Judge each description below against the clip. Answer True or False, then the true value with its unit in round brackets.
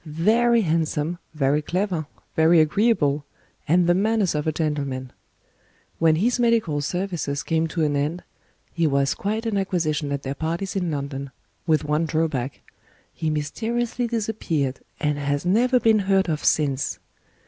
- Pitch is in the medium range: True (160 Hz)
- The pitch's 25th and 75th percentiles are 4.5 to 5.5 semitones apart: True (5.0 semitones)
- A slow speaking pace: False (150 wpm)